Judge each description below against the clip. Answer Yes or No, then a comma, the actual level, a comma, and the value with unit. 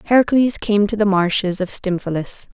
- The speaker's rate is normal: Yes, average, 160 wpm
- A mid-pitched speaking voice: No, high, 200 Hz